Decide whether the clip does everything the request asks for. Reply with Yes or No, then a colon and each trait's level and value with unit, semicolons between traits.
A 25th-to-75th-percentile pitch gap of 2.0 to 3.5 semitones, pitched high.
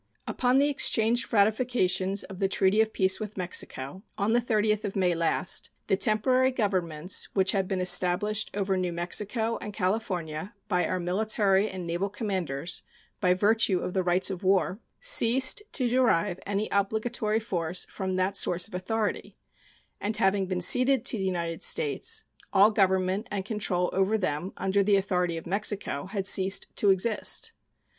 Yes: average, 2.9 semitones; high, 195 Hz